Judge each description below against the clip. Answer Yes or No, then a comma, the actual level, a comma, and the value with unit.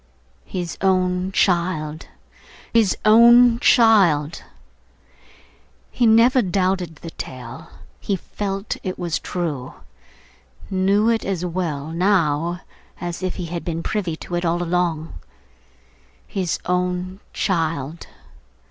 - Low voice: No, medium, 180 Hz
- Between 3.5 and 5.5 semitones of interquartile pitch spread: No, average, 2.8 semitones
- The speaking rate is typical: No, slow, 110 wpm